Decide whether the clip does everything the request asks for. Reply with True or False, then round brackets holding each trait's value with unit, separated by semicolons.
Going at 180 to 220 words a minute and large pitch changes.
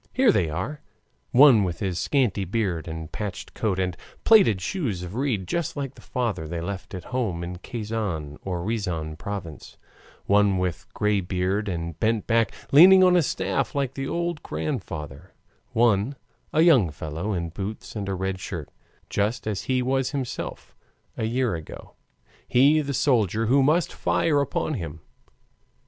False (160 wpm; 6.7 semitones)